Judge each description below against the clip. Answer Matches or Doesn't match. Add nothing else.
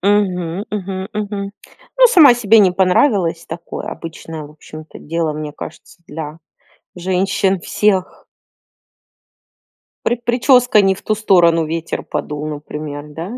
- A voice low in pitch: Doesn't match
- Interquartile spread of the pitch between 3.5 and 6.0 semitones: Matches